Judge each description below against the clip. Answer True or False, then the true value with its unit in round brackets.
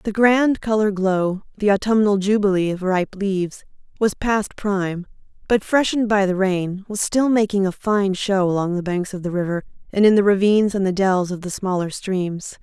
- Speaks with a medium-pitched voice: False (195 Hz)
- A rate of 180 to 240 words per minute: True (185 wpm)